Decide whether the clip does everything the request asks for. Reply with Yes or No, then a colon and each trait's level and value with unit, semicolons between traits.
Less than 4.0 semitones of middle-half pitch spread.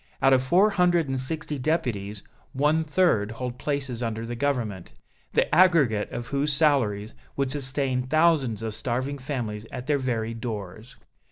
No: average, 4.6 semitones